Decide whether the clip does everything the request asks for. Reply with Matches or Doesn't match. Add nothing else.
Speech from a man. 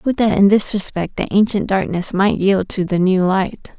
Doesn't match